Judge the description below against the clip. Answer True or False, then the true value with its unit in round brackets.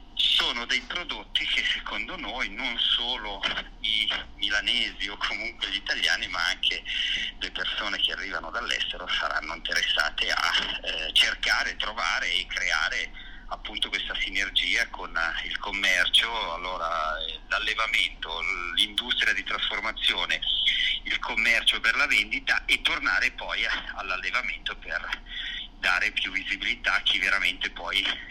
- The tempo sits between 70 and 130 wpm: True (120 wpm)